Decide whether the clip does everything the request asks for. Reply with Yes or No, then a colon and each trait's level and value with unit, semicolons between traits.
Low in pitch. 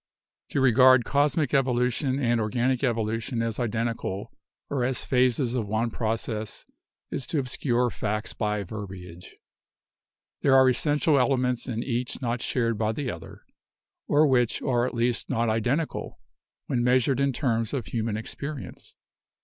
Yes: low, 120 Hz